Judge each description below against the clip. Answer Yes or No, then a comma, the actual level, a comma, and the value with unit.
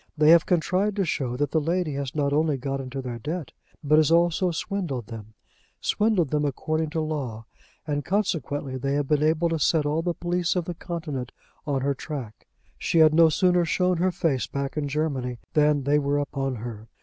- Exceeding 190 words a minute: Yes, average, 200 wpm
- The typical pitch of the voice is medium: Yes, medium, 150 Hz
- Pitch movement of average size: Yes, average, 3.5 semitones